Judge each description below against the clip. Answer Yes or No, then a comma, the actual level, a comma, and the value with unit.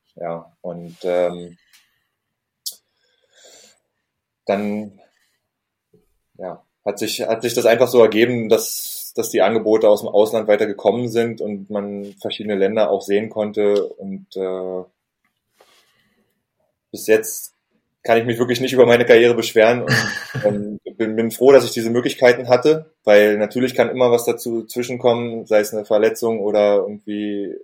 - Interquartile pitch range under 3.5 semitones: Yes, narrow, 2.6 semitones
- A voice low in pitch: Yes, low, 110 Hz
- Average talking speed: Yes, average, 140 wpm